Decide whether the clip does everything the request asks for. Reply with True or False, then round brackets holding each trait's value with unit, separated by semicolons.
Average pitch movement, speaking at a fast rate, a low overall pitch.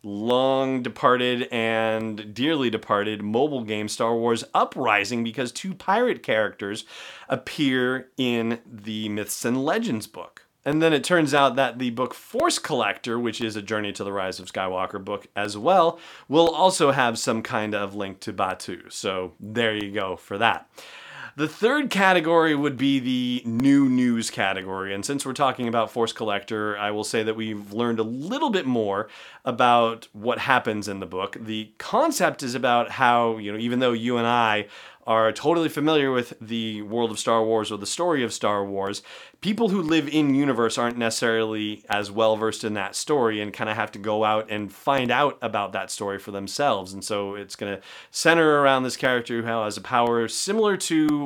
False (3.8 semitones; 185 wpm; 115 Hz)